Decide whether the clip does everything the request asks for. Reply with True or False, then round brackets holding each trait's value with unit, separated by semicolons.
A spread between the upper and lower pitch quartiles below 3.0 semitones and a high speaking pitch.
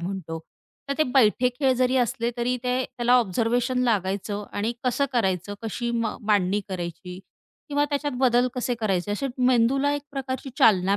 False (3.9 semitones; 235 Hz)